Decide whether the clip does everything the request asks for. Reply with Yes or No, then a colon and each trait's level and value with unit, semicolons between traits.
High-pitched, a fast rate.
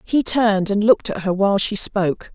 Yes: high, 205 Hz; fast, 230 wpm